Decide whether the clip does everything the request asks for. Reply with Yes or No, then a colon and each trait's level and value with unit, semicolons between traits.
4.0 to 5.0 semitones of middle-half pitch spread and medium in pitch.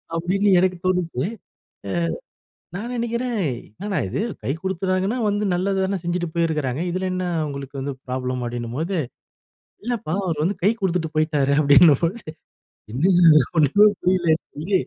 Yes: average, 4.4 semitones; medium, 175 Hz